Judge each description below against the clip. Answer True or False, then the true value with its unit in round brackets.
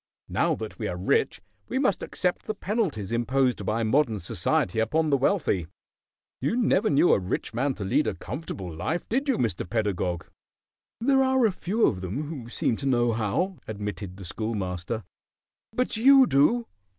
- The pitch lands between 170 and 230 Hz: False (125 Hz)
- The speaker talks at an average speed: True (170 wpm)